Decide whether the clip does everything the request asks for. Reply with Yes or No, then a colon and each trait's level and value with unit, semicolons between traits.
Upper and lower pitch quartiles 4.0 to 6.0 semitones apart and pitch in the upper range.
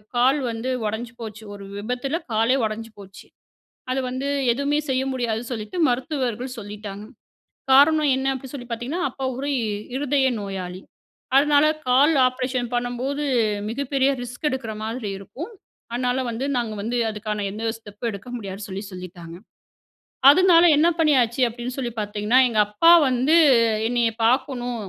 No: average, 3.5 semitones; high, 245 Hz